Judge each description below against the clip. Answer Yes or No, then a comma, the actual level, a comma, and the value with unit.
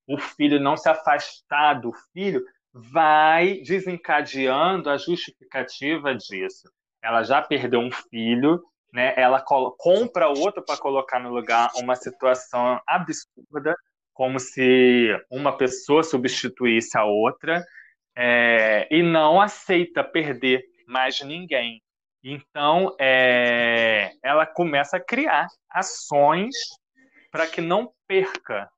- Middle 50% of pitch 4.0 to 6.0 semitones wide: Yes, wide, 5.6 semitones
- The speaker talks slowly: Yes, slow, 115 wpm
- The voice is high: No, medium, 145 Hz